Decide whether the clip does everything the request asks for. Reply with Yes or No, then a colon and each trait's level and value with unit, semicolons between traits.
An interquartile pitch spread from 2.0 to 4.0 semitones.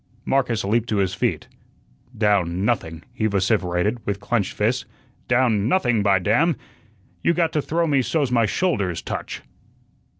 No: average, 4.5 semitones